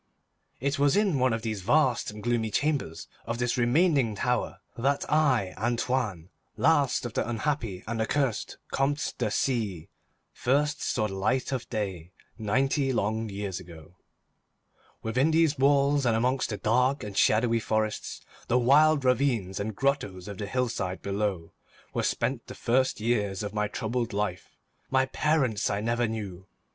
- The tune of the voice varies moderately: Yes, average, 4.5 semitones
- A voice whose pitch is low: Yes, low, 115 Hz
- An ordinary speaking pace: Yes, average, 155 wpm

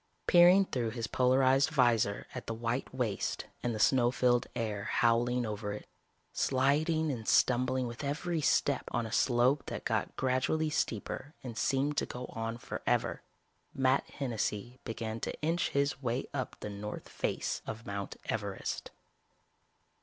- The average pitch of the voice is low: Yes, low, 125 Hz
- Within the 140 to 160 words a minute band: Yes, average, 150 wpm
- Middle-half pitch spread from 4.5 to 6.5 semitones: No, average, 3.3 semitones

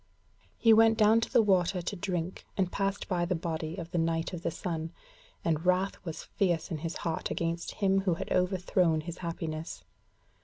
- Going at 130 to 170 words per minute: No, average, 190 wpm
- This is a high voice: No, medium, 175 Hz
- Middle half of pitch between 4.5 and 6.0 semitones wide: No, average, 2.7 semitones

